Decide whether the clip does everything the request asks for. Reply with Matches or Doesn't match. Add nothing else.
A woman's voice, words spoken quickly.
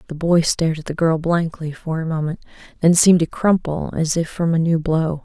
Matches